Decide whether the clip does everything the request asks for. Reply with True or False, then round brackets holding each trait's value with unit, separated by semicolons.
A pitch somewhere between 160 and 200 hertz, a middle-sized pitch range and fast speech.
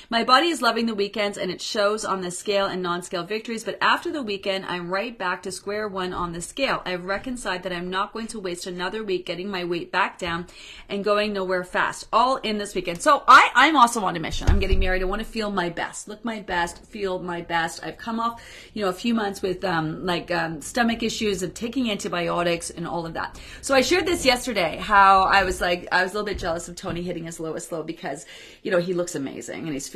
True (190 Hz; 3.5 semitones; 250 wpm)